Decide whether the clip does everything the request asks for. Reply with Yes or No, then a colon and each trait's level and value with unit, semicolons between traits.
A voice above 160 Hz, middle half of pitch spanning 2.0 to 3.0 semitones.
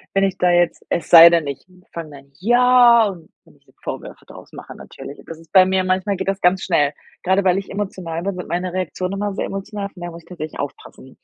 Yes: medium, 185 Hz; average, 2.7 semitones